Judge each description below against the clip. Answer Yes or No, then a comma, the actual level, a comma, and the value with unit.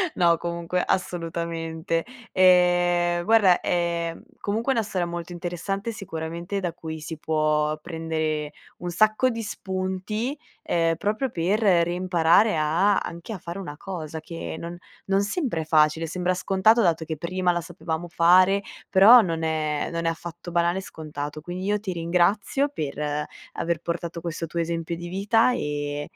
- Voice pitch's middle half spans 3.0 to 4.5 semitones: No, narrow, 2.6 semitones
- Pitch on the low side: No, medium, 175 Hz